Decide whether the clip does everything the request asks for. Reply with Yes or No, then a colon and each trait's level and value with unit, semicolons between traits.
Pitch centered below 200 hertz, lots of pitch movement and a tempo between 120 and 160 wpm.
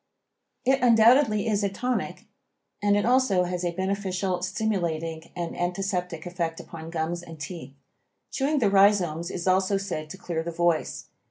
No: medium, 185 Hz; average, 3.2 semitones; average, 155 wpm